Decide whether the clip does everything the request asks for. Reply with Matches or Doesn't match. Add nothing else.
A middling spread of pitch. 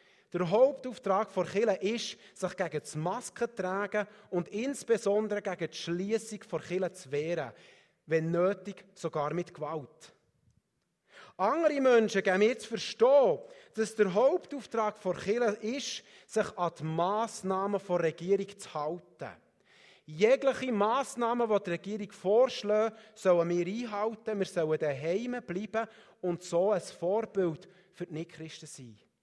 Matches